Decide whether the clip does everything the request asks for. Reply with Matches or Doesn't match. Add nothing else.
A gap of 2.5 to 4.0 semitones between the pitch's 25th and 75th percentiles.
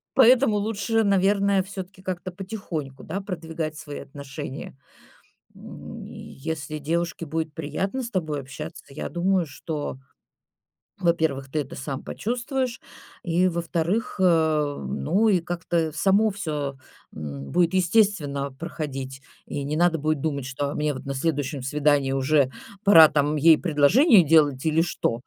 Doesn't match